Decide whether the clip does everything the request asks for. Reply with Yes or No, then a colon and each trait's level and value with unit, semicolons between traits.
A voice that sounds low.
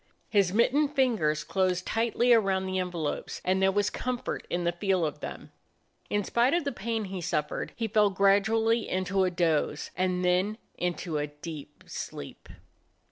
No: high, 190 Hz